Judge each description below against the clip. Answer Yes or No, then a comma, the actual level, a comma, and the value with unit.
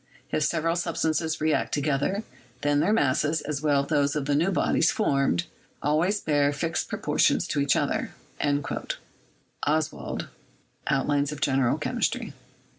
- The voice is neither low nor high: Yes, medium, 150 Hz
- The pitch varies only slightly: Yes, narrow, 2.1 semitones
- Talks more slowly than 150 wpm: Yes, slow, 135 wpm